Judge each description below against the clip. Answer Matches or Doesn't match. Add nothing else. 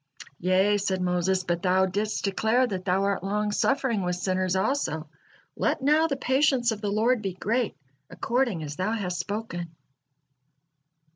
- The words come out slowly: Doesn't match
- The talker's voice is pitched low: Doesn't match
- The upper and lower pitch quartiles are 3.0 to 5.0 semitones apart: Matches